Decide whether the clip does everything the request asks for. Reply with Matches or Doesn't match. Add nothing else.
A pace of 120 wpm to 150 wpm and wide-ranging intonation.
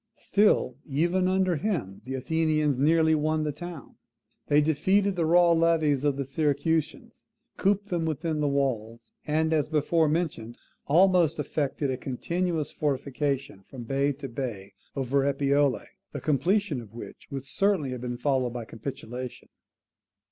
Doesn't match